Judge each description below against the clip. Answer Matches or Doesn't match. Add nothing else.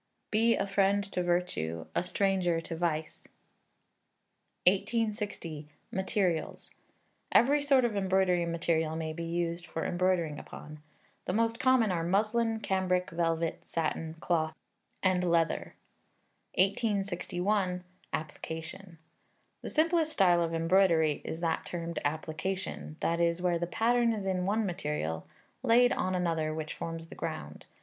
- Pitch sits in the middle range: Matches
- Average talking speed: Doesn't match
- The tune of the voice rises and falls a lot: Doesn't match